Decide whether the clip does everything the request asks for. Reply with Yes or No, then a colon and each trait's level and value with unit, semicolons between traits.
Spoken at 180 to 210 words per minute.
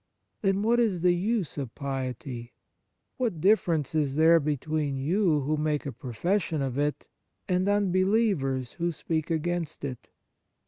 No: average, 140 wpm